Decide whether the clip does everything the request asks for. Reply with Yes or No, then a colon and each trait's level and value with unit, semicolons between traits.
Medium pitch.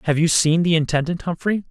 Yes: medium, 165 Hz